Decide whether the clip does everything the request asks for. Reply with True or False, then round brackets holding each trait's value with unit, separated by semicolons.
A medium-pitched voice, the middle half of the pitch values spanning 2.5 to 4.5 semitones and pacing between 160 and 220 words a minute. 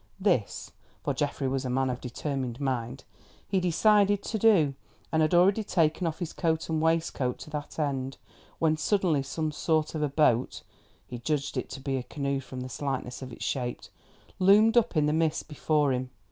True (150 Hz; 3.8 semitones; 175 wpm)